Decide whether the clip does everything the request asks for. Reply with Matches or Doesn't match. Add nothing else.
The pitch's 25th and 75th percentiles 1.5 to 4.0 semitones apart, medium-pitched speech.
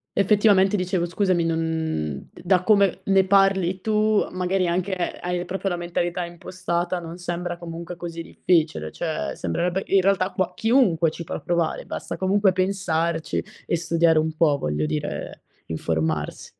Matches